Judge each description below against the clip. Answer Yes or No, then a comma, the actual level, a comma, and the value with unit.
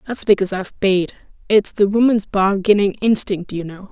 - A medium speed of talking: Yes, average, 170 wpm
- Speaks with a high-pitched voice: Yes, high, 200 Hz